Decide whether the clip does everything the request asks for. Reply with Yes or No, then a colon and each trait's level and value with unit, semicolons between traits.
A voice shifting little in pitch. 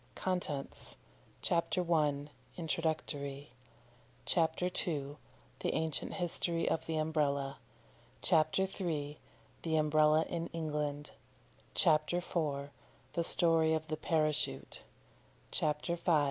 Yes: narrow, 2.1 semitones